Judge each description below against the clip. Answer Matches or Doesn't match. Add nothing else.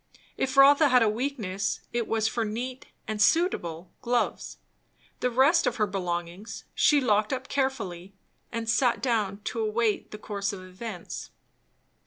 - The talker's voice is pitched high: Matches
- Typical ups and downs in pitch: Matches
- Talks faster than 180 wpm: Doesn't match